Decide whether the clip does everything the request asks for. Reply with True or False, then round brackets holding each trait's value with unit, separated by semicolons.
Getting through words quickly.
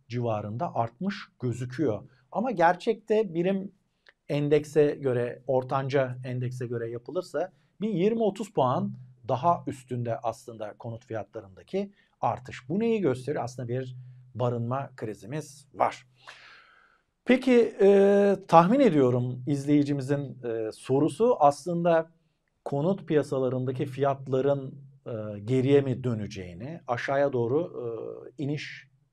False (100 wpm)